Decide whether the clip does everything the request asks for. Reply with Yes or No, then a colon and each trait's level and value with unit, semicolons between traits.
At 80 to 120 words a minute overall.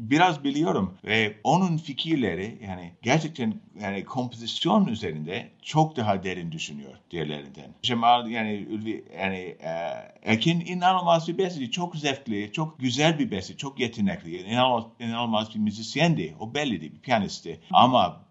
No: fast, 140 wpm